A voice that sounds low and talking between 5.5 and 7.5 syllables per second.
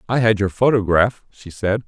No: low, 105 Hz; 4.9 syllables/s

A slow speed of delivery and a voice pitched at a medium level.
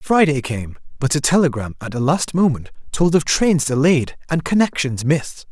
No: average, 175 wpm; medium, 145 Hz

